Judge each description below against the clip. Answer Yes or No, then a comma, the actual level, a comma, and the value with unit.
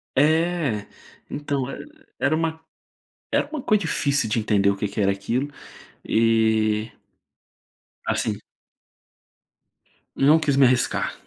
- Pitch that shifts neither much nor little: No, wide, 6.2 semitones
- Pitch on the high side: No, low, 135 Hz